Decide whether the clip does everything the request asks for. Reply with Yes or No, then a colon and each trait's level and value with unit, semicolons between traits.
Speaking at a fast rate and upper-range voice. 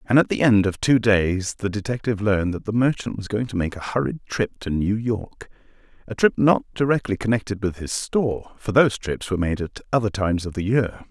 No: fast, 220 wpm; low, 105 Hz